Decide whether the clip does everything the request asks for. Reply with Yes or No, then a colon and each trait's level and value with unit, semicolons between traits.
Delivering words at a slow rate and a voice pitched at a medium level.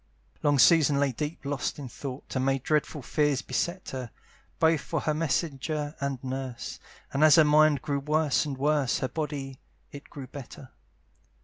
No: average, 170 wpm; medium, 145 Hz